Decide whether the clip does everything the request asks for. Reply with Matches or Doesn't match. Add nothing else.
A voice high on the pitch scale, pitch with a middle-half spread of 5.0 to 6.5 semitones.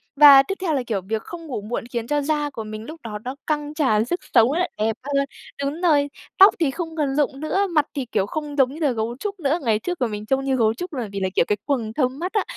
Matches